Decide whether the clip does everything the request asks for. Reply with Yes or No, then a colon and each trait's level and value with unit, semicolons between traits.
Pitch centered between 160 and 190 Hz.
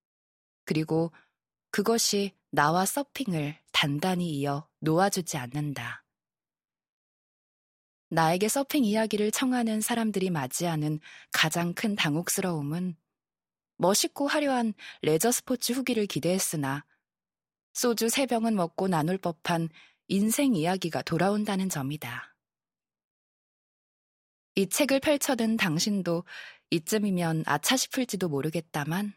Yes: medium, 185 Hz